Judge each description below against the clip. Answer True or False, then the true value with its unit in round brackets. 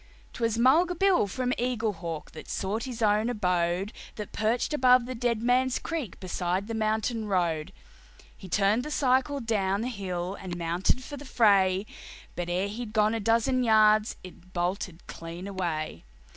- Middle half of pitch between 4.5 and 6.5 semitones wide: True (4.9 semitones)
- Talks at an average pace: True (160 wpm)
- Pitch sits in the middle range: False (215 Hz)